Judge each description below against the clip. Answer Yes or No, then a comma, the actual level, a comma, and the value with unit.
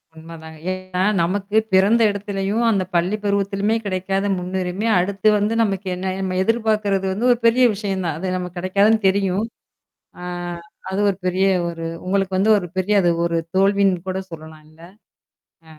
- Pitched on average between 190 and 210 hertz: Yes, high, 195 Hz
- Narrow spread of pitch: Yes, narrow, 1.9 semitones